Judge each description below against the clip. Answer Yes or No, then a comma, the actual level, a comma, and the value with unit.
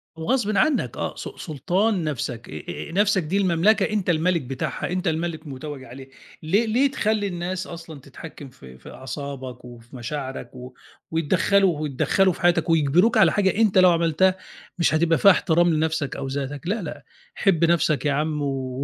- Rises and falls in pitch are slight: No, average, 5.1 semitones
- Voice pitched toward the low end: No, medium, 160 Hz